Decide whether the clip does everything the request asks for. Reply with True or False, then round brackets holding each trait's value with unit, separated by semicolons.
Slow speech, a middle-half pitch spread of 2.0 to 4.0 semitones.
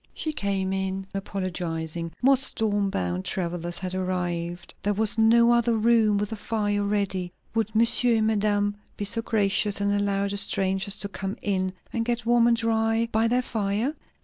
False (175 wpm; 2.9 semitones)